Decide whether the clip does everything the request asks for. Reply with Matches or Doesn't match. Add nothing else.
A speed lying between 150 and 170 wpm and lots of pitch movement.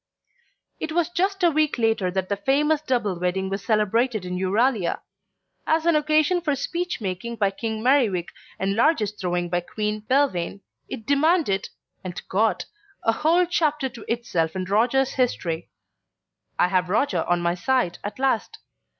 Matches